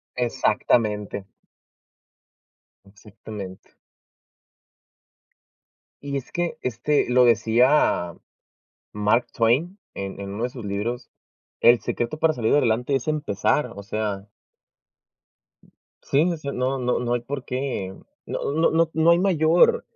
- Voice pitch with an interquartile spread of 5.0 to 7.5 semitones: Yes, wide, 5.4 semitones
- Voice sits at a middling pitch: No, low, 125 Hz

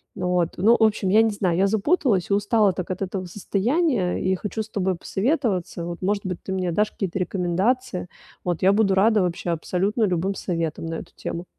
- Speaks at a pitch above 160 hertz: Yes, high, 190 Hz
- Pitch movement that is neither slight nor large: Yes, average, 3.1 semitones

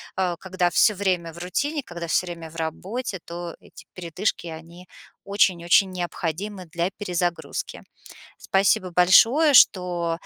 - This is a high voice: No, medium, 180 Hz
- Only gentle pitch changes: Yes, narrow, 2.3 semitones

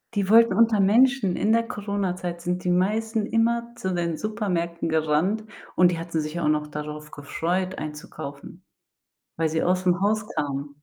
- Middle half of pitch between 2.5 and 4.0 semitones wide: No, average, 5.2 semitones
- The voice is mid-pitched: Yes, medium, 180 Hz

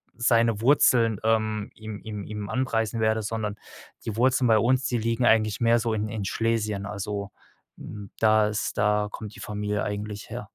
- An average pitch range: No, narrow, 1.6 semitones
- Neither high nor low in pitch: No, low, 110 Hz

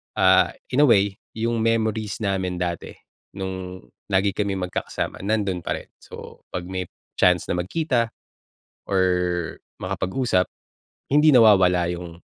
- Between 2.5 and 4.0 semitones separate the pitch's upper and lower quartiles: Yes, average, 3.5 semitones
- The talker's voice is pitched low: Yes, very low, 95 Hz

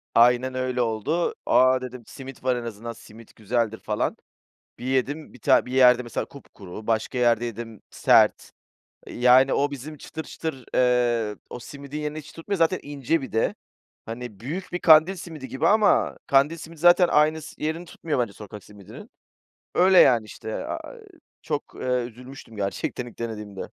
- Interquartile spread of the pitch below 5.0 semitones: Yes, average, 4.5 semitones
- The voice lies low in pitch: Yes, low, 125 Hz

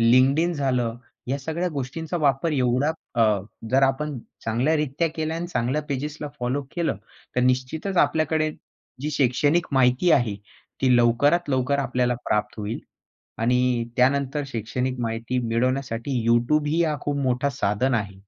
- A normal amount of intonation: Yes, average, 3.5 semitones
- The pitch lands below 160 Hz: Yes, low, 135 Hz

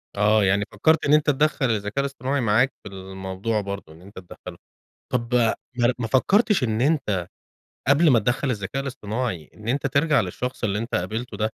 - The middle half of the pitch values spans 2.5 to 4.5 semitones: No, average, 5.3 semitones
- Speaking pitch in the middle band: No, low, 115 Hz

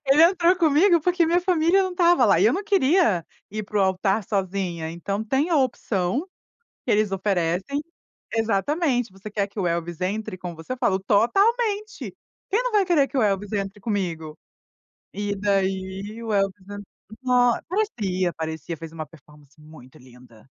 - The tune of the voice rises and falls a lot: Yes, wide, 8.6 semitones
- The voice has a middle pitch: No, high, 205 Hz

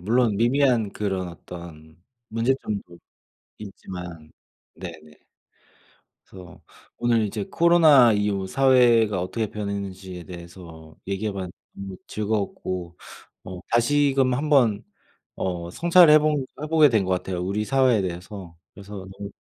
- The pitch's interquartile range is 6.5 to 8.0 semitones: No, average, 5.3 semitones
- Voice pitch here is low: Yes, low, 100 Hz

